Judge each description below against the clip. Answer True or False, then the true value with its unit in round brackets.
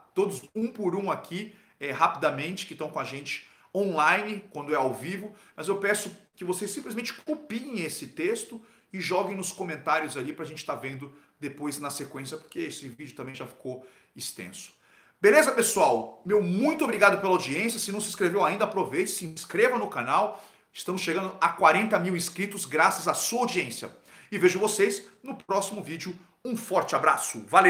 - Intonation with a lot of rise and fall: False (5.0 semitones)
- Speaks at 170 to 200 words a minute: True (180 wpm)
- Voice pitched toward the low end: False (190 Hz)